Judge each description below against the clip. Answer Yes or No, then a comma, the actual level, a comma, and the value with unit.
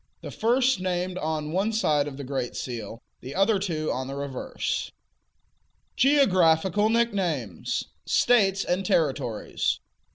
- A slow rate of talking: Yes, slow, 125 wpm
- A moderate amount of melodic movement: No, wide, 6.3 semitones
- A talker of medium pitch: Yes, medium, 175 Hz